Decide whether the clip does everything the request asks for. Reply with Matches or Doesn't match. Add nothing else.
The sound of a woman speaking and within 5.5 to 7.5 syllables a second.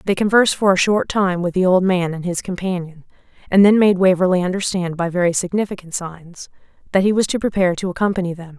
Matches